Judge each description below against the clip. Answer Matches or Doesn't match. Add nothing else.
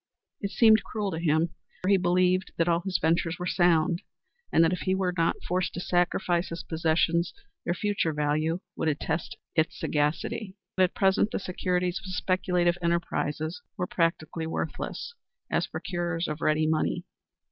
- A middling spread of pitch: Doesn't match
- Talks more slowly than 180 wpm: Matches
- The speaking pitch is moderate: Matches